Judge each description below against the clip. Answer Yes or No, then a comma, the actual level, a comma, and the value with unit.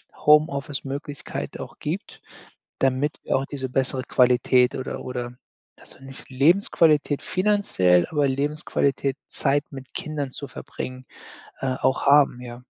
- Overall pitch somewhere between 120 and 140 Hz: Yes, low, 135 Hz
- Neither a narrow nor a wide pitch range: No, narrow, 2.2 semitones